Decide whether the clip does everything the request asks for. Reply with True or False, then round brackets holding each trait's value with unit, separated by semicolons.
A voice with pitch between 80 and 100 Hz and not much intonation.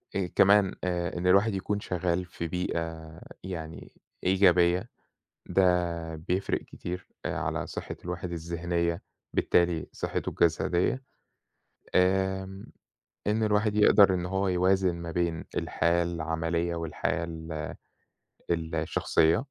True (90 Hz; 2.2 semitones)